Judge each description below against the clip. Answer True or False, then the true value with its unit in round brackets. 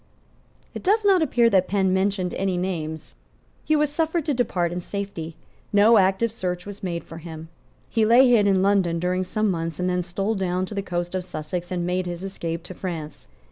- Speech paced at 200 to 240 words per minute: True (205 wpm)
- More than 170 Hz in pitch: True (185 Hz)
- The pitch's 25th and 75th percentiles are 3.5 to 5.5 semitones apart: False (2.8 semitones)